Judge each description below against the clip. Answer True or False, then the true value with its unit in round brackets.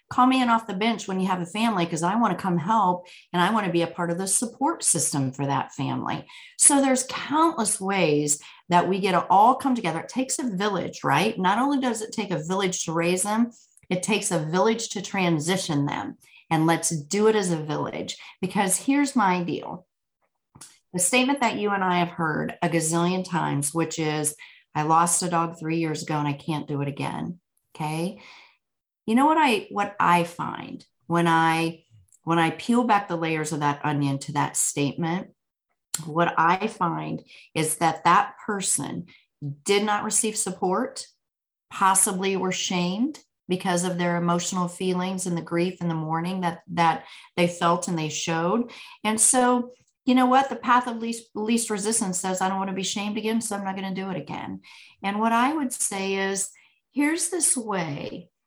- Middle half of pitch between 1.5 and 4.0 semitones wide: False (4.8 semitones)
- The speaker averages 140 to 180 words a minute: False (195 wpm)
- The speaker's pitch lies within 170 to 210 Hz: True (185 Hz)